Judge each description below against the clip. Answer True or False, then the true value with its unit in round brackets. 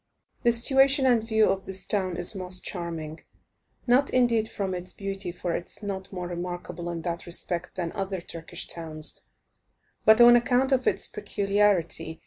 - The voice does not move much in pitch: False (4.2 semitones)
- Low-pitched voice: False (190 Hz)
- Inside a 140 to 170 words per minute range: True (165 wpm)